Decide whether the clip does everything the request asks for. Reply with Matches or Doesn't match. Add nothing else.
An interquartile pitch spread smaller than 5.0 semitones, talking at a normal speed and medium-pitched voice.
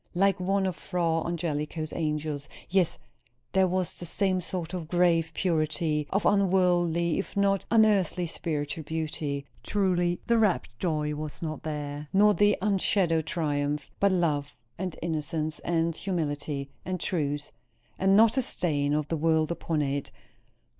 Matches